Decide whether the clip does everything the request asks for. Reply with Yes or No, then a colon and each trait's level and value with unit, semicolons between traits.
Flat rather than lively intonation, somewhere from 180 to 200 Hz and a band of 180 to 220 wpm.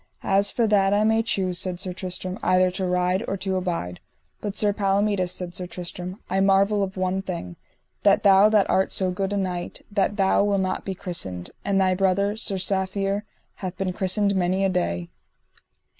Yes: narrow, 1.6 semitones; high, 190 Hz; average, 190 wpm